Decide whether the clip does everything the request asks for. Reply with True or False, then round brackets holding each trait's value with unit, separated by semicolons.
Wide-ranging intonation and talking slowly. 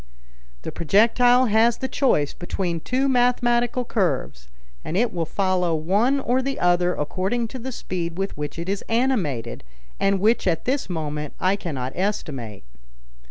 False (6.6 semitones; 155 wpm)